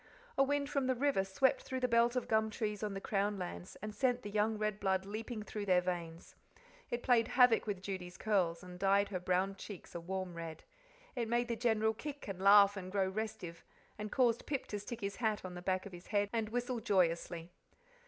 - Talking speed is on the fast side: Yes, fast, 220 wpm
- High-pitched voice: Yes, high, 205 Hz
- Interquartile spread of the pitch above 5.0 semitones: No, average, 3.7 semitones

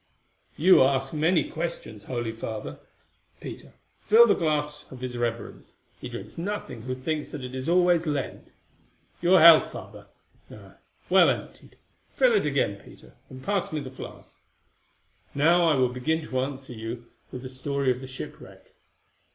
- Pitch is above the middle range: No, medium, 140 Hz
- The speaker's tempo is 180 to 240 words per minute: No, average, 160 wpm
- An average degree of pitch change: Yes, average, 4.5 semitones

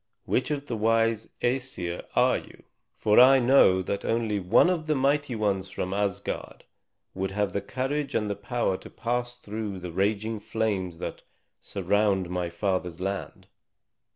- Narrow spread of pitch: No, average, 4.3 semitones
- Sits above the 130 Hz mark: No, low, 105 Hz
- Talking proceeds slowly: No, average, 155 wpm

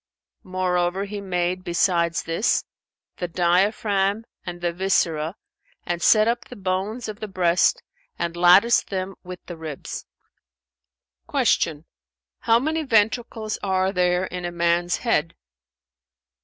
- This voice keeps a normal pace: No, slow, 125 wpm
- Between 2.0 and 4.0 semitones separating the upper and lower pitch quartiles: Yes, average, 2.9 semitones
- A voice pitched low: No, medium, 185 Hz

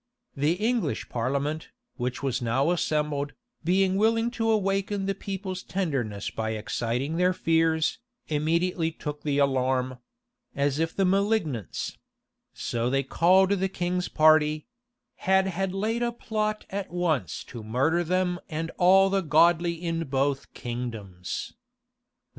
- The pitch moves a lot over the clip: Yes, wide, 5.7 semitones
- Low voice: No, medium, 165 Hz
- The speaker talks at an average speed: No, slow, 130 wpm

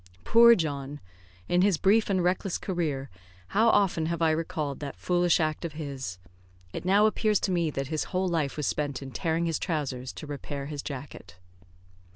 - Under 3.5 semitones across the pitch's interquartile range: No, average, 4.3 semitones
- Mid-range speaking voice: Yes, medium, 160 Hz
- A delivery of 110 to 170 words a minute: No, average, 185 wpm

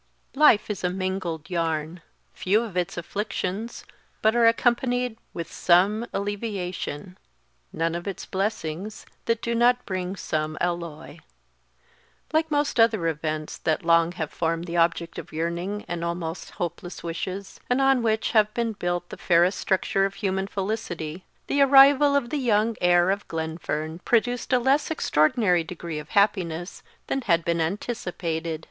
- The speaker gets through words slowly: No, average, 155 wpm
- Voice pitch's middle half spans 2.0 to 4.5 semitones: No, average, 5.1 semitones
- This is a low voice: No, medium, 185 Hz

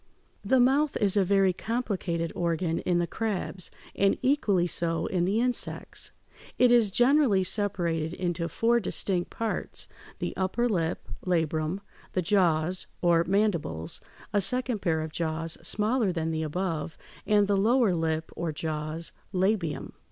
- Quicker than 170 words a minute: No, average, 145 wpm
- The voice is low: No, medium, 185 Hz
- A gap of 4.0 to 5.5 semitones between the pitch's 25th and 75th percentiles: Yes, average, 4.3 semitones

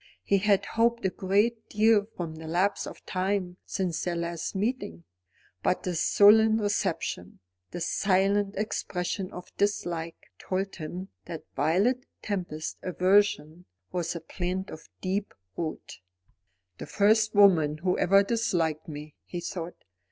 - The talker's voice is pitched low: No, medium, 185 Hz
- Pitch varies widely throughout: No, average, 3.2 semitones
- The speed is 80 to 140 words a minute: Yes, slow, 135 wpm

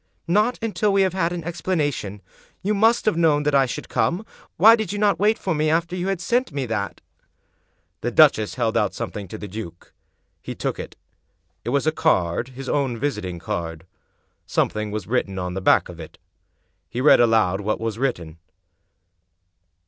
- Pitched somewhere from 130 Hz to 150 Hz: Yes, medium, 140 Hz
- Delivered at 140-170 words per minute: No, average, 185 wpm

